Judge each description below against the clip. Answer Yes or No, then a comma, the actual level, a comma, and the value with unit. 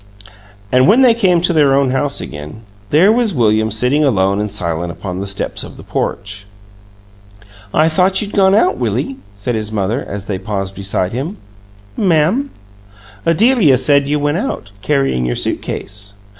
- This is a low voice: Yes, low, 130 Hz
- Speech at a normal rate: Yes, average, 170 wpm